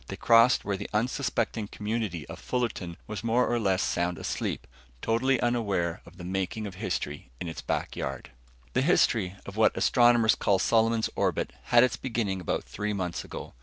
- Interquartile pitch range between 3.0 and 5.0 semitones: Yes, average, 4.1 semitones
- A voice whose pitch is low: Yes, low, 105 Hz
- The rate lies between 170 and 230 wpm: Yes, average, 175 wpm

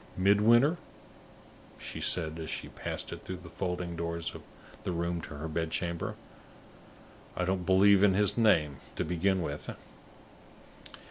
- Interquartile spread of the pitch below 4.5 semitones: Yes, average, 2.8 semitones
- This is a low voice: Yes, very low, 90 Hz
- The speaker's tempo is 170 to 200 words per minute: No, average, 140 wpm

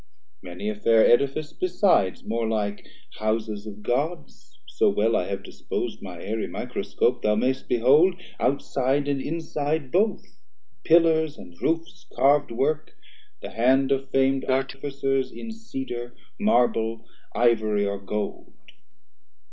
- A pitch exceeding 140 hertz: No, low, 130 Hz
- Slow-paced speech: Yes, slow, 125 wpm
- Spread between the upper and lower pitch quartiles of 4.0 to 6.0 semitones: Yes, average, 5.0 semitones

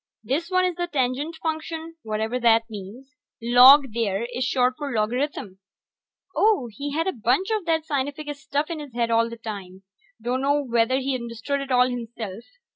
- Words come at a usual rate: Yes, average, 175 wpm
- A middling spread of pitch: Yes, average, 4.2 semitones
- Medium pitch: No, very high, 255 Hz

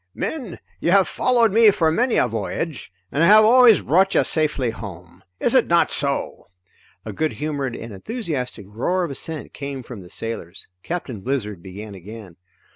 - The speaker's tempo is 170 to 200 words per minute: Yes, average, 175 wpm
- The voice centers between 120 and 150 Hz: Yes, medium, 140 Hz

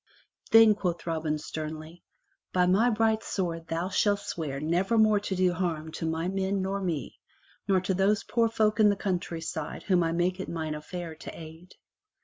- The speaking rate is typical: Yes, average, 180 wpm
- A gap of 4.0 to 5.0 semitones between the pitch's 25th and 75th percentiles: No, average, 3.5 semitones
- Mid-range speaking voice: Yes, medium, 180 Hz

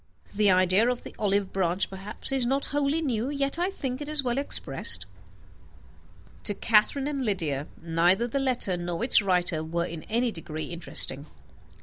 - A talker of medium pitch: No, high, 210 Hz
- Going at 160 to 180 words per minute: Yes, average, 165 wpm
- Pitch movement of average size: No, wide, 7.3 semitones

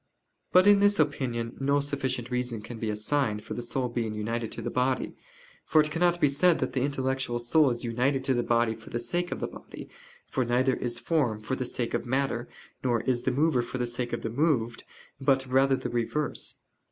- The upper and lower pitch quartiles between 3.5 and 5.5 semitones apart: No, average, 2.9 semitones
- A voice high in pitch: No, low, 125 Hz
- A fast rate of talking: Yes, fast, 215 wpm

